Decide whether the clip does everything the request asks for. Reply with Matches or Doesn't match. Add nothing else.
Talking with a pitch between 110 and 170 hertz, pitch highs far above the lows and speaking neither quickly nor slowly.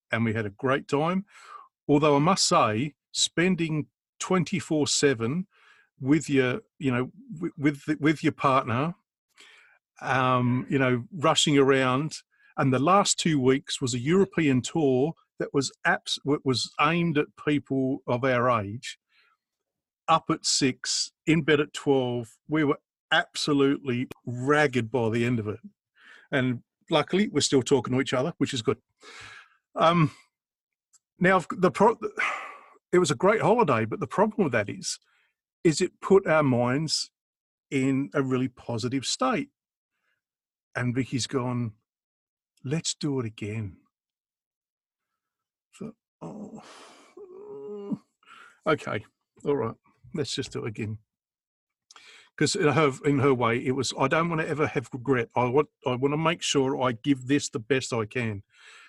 Doesn't match